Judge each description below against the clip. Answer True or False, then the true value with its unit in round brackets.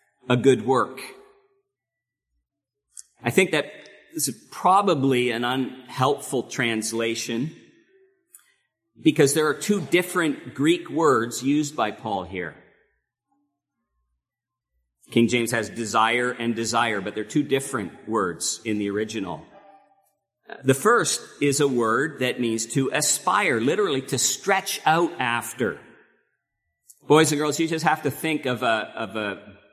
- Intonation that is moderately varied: False (5.9 semitones)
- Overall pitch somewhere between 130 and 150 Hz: True (135 Hz)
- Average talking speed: False (125 wpm)